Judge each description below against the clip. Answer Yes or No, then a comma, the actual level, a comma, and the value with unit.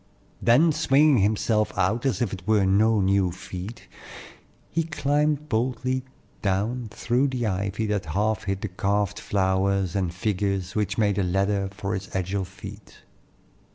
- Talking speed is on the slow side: No, average, 150 wpm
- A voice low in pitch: Yes, low, 100 Hz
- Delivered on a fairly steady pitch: No, average, 3.4 semitones